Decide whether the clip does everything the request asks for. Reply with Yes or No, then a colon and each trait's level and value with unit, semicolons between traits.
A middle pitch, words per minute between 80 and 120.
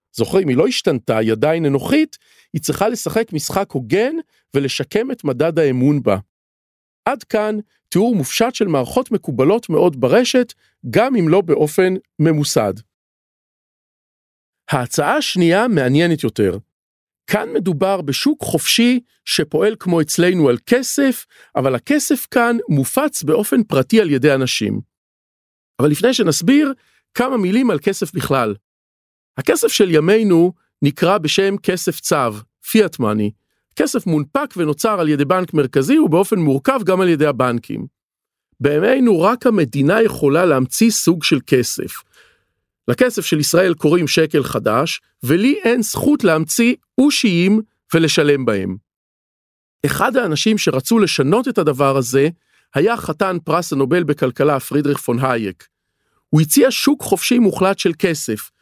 No: medium, 175 Hz; average, 130 wpm